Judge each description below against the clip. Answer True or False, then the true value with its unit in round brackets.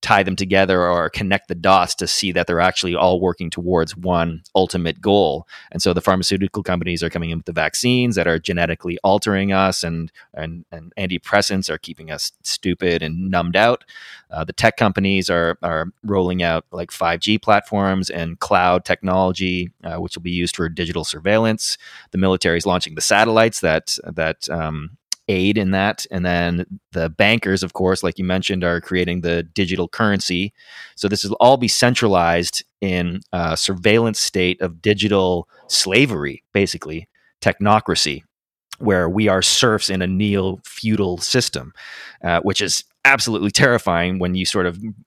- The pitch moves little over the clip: True (2.3 semitones)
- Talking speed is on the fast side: False (170 wpm)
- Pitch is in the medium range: False (95 Hz)